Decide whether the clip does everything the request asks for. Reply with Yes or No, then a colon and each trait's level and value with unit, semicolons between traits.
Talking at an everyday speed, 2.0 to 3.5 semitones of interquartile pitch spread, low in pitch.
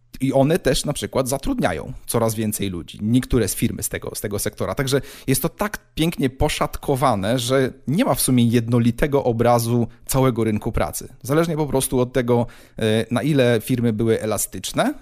No: fast, 170 wpm; average, 3.0 semitones; low, 120 Hz